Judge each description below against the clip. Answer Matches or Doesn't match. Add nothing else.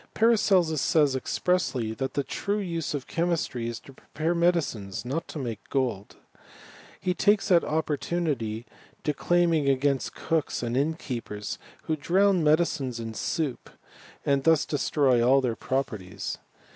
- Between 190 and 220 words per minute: Doesn't match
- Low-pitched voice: Doesn't match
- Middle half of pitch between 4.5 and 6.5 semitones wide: Matches